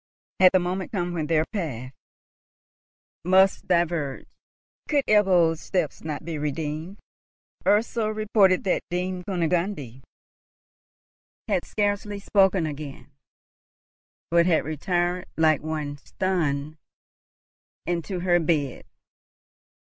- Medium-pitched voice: Yes, medium, 175 Hz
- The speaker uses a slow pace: Yes, slow, 100 wpm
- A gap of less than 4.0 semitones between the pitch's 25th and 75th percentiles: Yes, average, 3.6 semitones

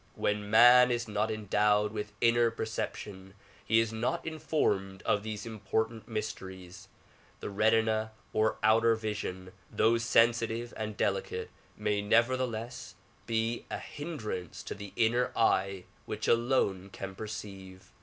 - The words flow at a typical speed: No, slow, 125 wpm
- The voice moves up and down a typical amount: No, narrow, 2.1 semitones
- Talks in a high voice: No, low, 110 Hz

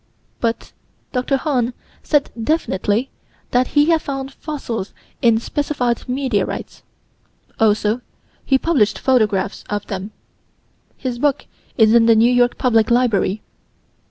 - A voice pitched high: Yes, high, 245 Hz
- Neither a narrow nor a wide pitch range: Yes, average, 3.5 semitones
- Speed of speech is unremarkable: No, slow, 120 wpm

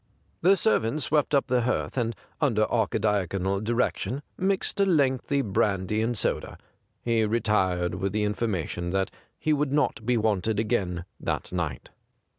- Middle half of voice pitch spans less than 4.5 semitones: No, average, 5.1 semitones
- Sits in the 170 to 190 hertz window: No, low, 110 Hz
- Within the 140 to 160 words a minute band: Yes, average, 150 wpm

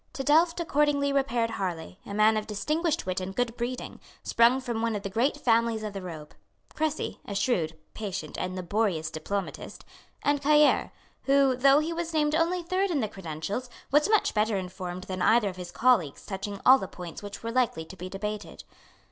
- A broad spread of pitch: Yes, wide, 6.7 semitones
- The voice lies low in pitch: No, high, 225 Hz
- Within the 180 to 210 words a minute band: Yes, average, 190 wpm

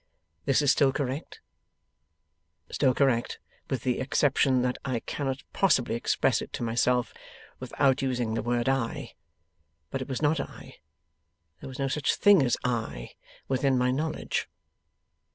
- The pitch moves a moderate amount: No, narrow, 2.1 semitones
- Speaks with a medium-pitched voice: No, low, 130 Hz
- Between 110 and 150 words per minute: Yes, average, 145 wpm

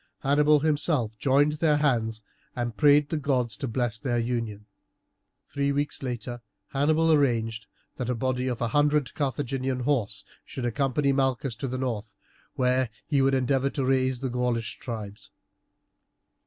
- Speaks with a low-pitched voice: Yes, low, 130 Hz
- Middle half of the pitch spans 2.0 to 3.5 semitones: Yes, average, 3.0 semitones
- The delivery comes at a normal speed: Yes, average, 150 wpm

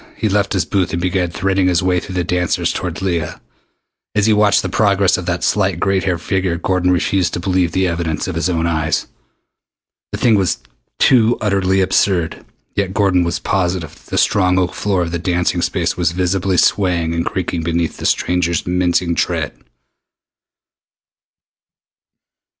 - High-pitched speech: No, very low, 90 Hz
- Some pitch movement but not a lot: No, narrow, 2.0 semitones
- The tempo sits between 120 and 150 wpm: No, average, 170 wpm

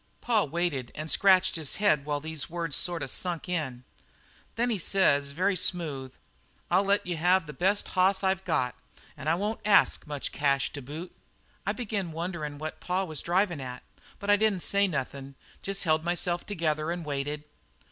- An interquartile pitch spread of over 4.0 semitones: Yes, average, 4.4 semitones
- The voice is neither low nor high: Yes, medium, 170 Hz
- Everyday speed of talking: Yes, average, 180 wpm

